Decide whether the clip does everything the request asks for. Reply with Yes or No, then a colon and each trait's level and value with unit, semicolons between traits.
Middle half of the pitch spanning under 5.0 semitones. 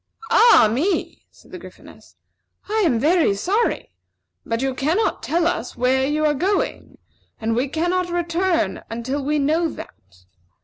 No: wide, 5.6 semitones